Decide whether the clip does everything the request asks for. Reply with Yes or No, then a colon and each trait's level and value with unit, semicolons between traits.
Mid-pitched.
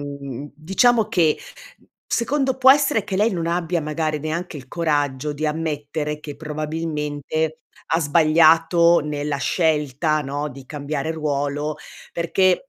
Yes: medium, 155 Hz